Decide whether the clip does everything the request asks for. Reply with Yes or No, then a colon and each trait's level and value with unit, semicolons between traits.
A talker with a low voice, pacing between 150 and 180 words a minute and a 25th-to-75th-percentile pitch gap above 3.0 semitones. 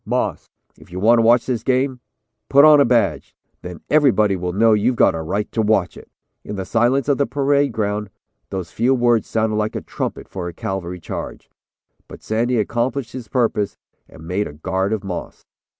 No: low, 110 Hz; average, 200 wpm; average, 4.4 semitones